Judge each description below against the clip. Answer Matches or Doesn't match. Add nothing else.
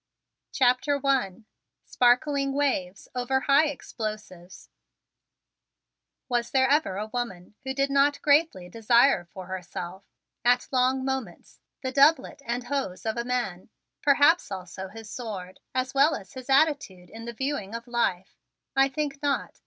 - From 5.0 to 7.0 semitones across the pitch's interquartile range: Matches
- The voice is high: Matches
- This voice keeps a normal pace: Matches